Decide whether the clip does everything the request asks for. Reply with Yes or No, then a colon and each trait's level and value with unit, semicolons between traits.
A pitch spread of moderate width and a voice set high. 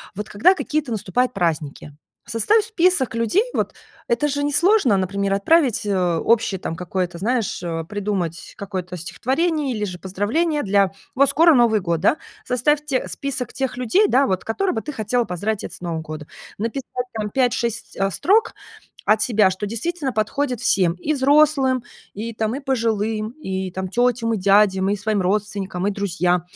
No: wide, 5.8 semitones; high, 220 Hz